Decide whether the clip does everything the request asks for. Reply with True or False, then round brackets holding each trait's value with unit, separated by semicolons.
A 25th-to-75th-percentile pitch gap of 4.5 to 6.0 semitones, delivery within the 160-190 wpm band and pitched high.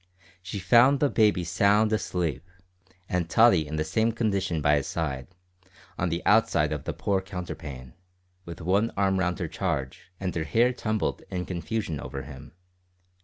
False (5.0 semitones; 165 wpm; 90 Hz)